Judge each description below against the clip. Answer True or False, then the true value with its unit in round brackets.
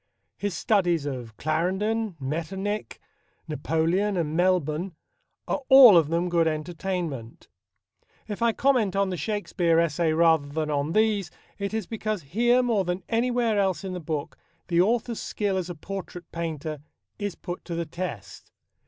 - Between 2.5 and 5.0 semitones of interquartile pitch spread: True (4.3 semitones)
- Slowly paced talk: False (155 wpm)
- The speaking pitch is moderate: True (180 Hz)